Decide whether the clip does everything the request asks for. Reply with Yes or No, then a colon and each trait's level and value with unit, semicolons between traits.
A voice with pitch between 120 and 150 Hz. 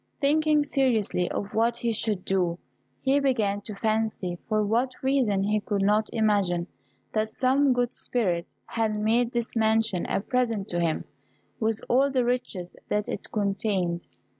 No: high, 220 Hz